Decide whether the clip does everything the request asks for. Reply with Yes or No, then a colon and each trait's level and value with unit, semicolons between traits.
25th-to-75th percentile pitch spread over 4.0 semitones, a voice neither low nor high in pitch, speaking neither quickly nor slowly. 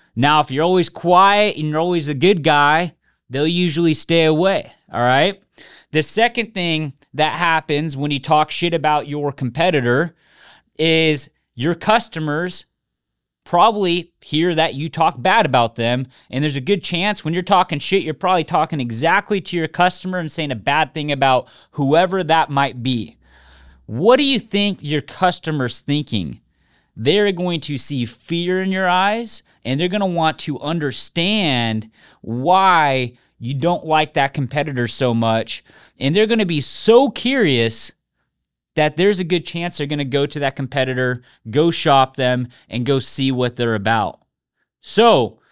Yes: average, 5.2 semitones; medium, 155 Hz; average, 165 wpm